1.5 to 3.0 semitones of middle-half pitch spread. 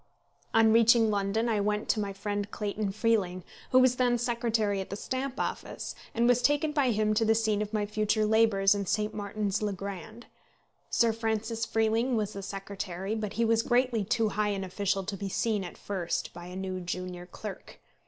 Yes: narrow, 2.4 semitones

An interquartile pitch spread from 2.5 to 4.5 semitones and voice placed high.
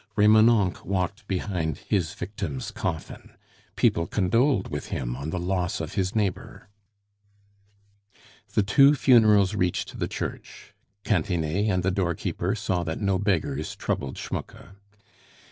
No: average, 3.4 semitones; very low, 95 Hz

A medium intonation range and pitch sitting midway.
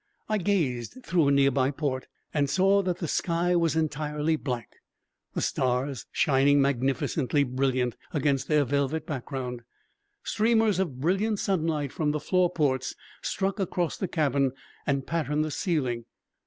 Yes: average, 4.3 semitones; medium, 150 Hz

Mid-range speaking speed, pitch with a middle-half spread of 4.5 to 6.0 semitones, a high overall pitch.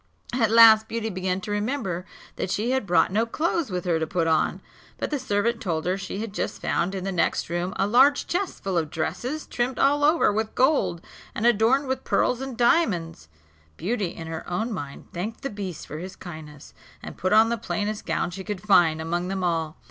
No: fast, 210 wpm; average, 5.1 semitones; high, 200 Hz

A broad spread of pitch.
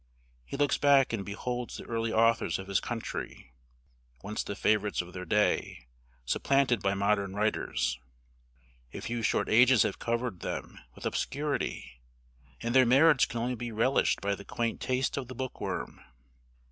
No: average, 4.0 semitones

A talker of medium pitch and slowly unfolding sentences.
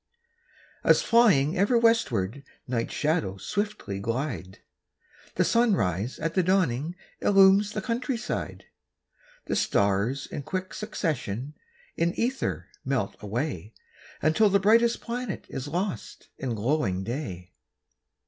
Yes: medium, 160 Hz; slow, 110 wpm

